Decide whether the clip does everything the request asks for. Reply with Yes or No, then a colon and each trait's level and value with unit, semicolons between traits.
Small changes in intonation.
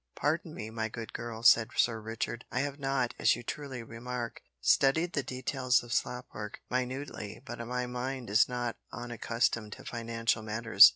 Yes: narrow, 2.1 semitones